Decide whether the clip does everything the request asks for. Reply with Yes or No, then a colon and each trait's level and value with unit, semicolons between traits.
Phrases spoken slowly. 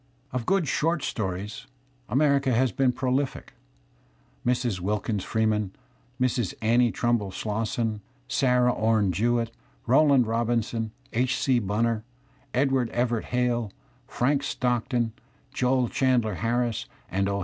Yes: slow, 115 wpm